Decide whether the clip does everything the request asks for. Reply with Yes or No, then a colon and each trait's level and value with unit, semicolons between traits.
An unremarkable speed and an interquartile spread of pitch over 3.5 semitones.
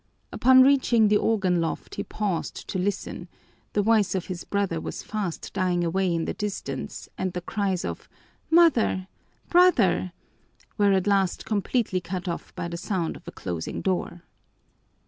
No: average, 160 wpm; average, 3.1 semitones